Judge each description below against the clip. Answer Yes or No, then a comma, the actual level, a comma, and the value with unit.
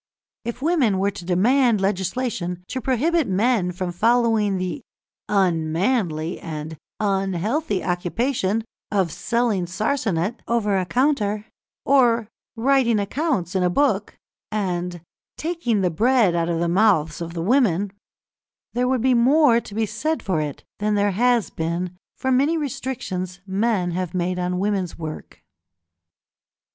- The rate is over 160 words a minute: No, slow, 135 wpm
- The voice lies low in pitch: No, high, 205 Hz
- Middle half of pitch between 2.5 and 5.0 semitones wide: No, wide, 5.4 semitones